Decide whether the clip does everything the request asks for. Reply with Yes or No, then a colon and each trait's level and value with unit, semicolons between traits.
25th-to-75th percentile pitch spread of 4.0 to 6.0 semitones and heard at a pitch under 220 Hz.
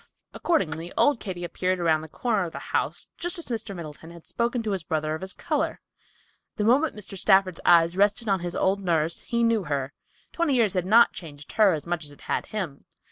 Yes: average, 5.3 semitones; medium, 185 Hz